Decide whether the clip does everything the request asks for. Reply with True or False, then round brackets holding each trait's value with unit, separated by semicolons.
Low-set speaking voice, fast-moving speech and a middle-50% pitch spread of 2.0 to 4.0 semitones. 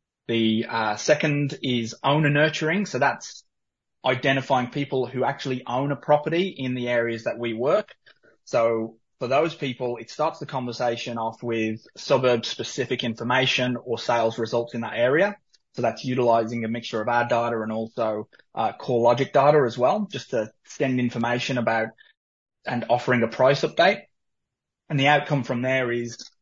False (125 Hz; 165 wpm; 2.9 semitones)